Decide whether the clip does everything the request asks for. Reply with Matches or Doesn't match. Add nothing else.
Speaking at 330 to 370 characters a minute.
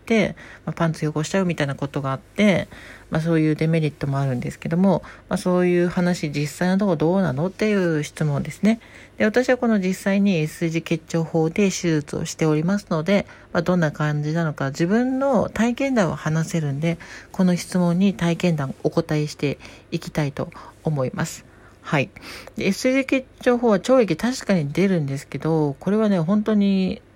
Matches